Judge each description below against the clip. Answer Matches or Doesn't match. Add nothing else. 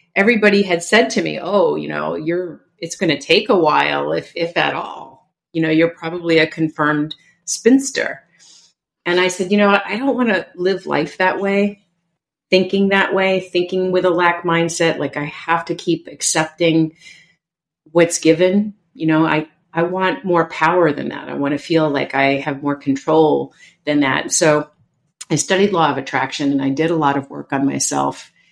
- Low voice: Doesn't match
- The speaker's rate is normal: Matches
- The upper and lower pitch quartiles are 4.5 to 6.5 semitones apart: Doesn't match